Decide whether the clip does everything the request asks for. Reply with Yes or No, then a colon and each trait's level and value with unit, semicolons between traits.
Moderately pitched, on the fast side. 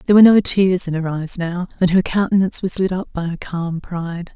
Yes: medium, 180 Hz; fast, 250 wpm